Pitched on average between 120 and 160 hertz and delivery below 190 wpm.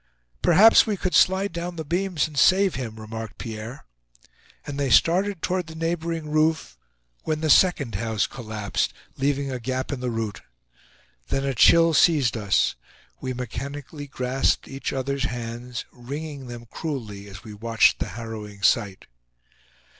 Yes: low, 135 Hz; average, 150 wpm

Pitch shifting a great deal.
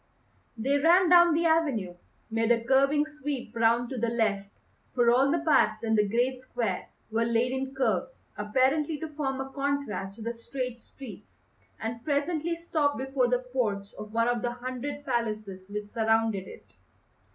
No: average, 4.0 semitones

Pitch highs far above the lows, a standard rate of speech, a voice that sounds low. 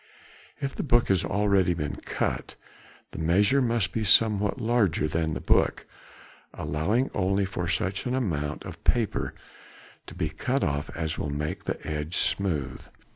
Yes: wide, 6.1 semitones; average, 150 wpm; very low, 95 Hz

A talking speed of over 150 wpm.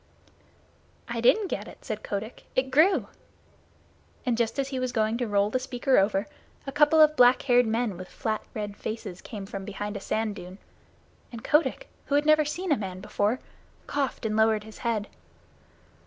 Yes: average, 185 wpm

